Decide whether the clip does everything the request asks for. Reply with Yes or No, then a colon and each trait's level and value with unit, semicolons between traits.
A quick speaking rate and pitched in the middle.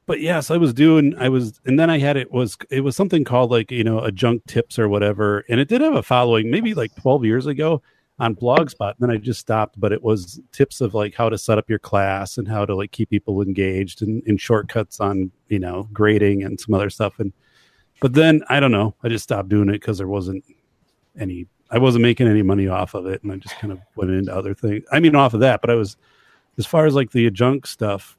No: fast, 260 wpm; low, 110 Hz